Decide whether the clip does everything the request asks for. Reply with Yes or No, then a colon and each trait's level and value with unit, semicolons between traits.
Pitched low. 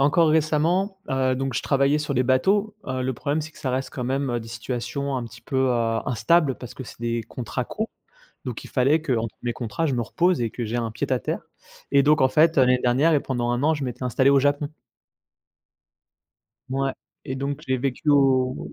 Yes: low, 130 Hz